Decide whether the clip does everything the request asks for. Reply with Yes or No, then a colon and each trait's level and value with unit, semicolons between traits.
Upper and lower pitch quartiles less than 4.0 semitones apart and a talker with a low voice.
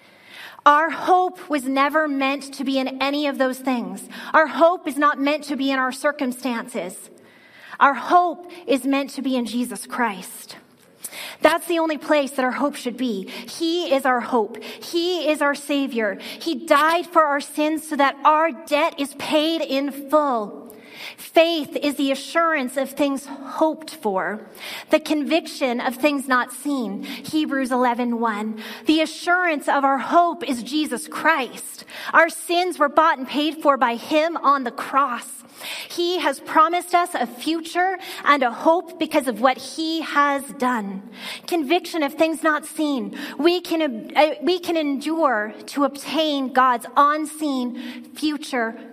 No: average, 3.5 semitones; very high, 285 Hz